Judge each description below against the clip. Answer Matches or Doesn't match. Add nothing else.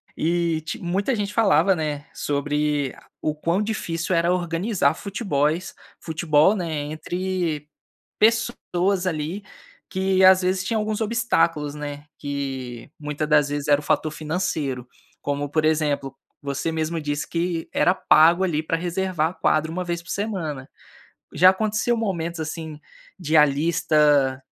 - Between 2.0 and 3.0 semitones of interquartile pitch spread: Doesn't match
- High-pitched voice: Doesn't match